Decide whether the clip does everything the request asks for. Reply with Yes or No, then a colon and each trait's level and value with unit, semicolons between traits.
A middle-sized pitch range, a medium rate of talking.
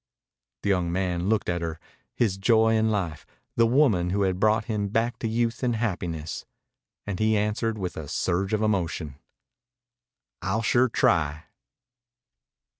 Yes: average, 4.1 semitones; average, 150 wpm